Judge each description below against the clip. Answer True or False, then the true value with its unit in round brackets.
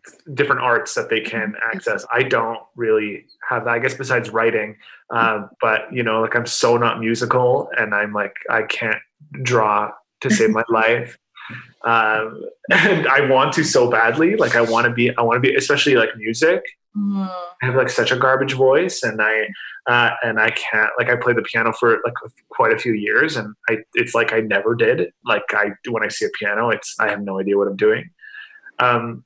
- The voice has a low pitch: True (120 Hz)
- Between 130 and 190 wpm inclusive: False (205 wpm)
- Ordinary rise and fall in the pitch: False (8.7 semitones)